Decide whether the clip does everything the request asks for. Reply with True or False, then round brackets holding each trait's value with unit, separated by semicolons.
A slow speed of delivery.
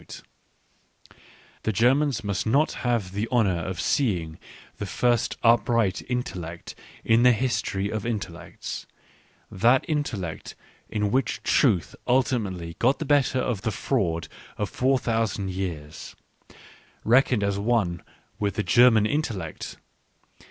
True (125 wpm)